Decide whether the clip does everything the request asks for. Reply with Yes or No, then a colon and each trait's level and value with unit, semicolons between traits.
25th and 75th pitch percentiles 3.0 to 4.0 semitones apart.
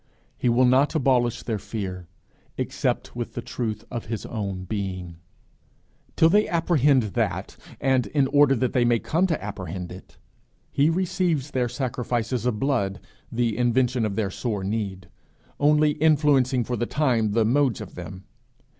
No: average, 4.9 semitones